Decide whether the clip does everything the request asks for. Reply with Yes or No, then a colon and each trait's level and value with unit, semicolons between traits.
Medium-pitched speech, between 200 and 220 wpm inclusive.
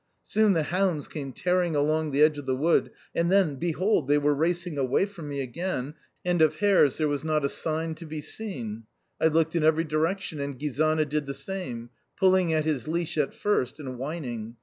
Yes: medium, 155 Hz; fast, 205 wpm